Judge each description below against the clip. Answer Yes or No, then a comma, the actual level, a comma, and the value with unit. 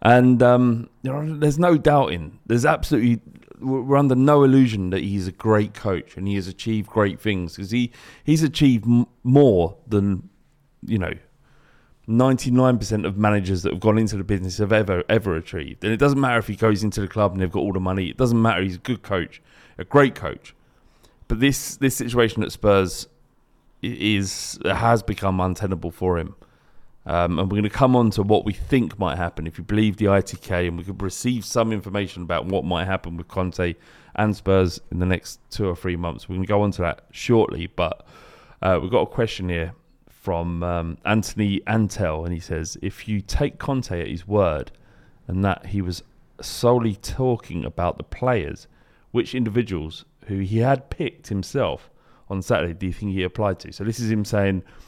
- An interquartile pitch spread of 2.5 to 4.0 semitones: No, average, 4.5 semitones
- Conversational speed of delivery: Yes, average, 195 wpm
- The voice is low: Yes, low, 105 Hz